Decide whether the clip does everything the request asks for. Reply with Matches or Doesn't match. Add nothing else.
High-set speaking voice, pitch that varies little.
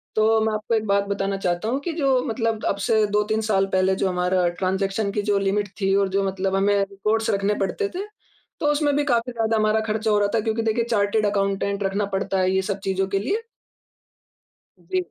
Matches